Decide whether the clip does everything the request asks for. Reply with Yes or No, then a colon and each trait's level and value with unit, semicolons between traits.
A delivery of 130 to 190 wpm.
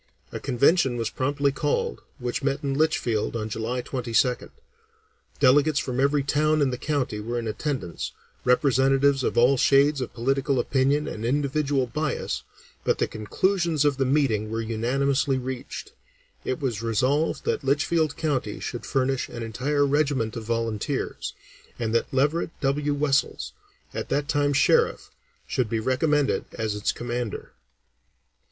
Yes: average, 145 wpm